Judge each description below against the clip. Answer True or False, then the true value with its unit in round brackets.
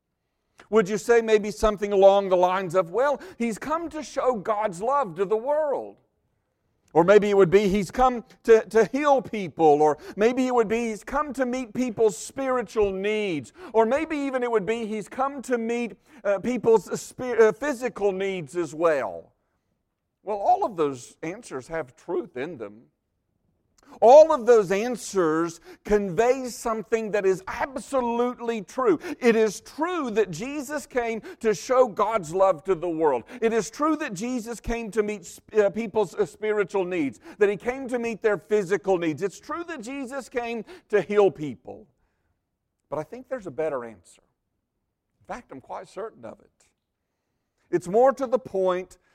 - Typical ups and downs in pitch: True (4.3 semitones)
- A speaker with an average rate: True (170 wpm)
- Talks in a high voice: True (220 Hz)